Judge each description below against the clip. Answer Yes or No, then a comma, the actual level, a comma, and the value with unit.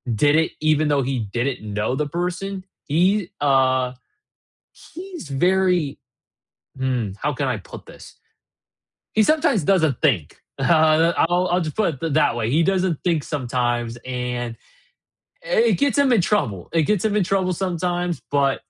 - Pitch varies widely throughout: Yes, wide, 6.0 semitones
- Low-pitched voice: No, medium, 155 Hz